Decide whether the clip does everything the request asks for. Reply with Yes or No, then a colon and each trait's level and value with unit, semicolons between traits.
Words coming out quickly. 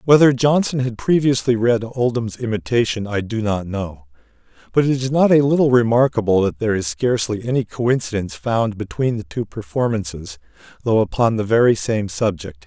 No: average, 165 wpm